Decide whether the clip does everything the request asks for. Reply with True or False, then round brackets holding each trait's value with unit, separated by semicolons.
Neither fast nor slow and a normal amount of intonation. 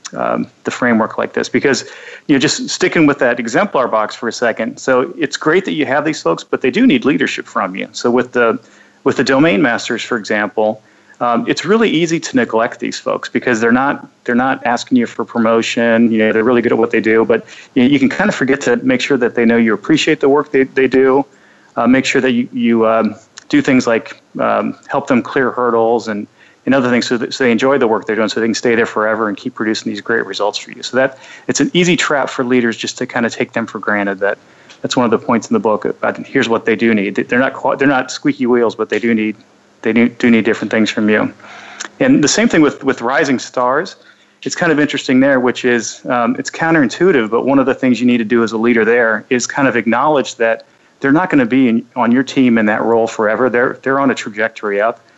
False (250 wpm; 3.2 semitones)